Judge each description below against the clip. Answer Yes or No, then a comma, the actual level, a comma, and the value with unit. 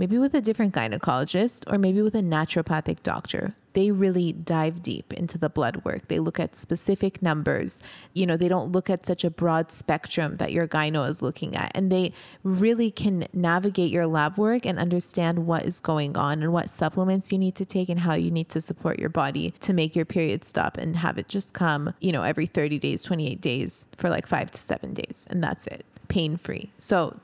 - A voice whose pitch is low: No, medium, 170 Hz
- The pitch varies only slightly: No, average, 3.0 semitones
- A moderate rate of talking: No, fast, 215 wpm